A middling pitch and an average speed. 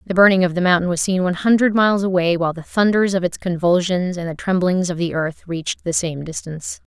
No: medium, 180 Hz; fast, 235 wpm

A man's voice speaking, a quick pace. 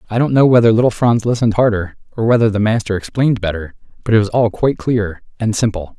Yes: male; fast, 220 wpm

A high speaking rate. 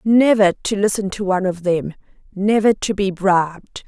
No: average, 170 wpm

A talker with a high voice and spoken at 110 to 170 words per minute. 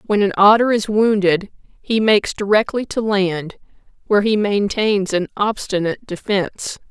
Yes: high, 205 Hz; average, 140 wpm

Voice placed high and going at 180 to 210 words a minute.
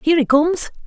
Yes: very high, 305 Hz; fast, 205 wpm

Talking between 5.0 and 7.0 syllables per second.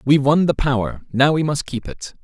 Yes: 5.6 syllables/s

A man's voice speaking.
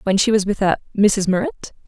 No: female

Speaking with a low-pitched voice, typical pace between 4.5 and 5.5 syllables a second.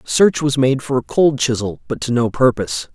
Yes: low, 130 Hz; 5.0 syllables/s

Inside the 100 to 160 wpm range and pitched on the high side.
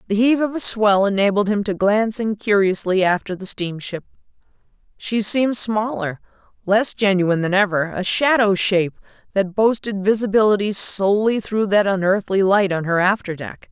Yes: average, 155 wpm; high, 200 Hz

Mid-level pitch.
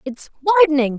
No: very high, 260 Hz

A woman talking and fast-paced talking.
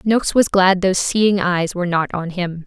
Yes: female; fast, 225 wpm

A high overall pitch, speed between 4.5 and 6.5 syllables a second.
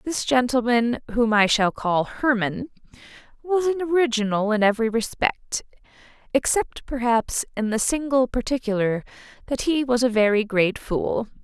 Yes: high, 240 Hz; 4.6 syllables/s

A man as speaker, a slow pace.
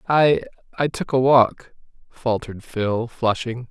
Yes: male; slow, 115 wpm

